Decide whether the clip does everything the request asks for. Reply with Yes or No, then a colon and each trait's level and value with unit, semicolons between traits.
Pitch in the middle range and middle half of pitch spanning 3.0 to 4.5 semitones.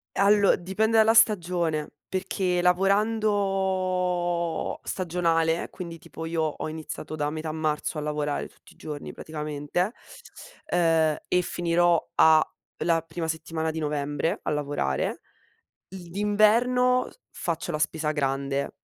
Yes: medium, 170 Hz; average, 3.4 semitones